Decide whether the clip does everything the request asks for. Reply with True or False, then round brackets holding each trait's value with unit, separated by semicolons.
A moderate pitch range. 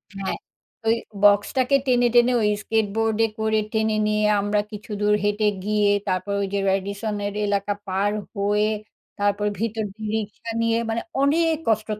False (1.6 semitones)